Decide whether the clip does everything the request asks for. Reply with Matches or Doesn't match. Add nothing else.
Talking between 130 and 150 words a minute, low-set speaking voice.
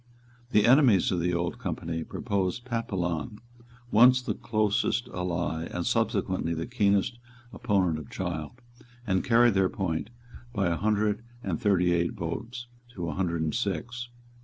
Matches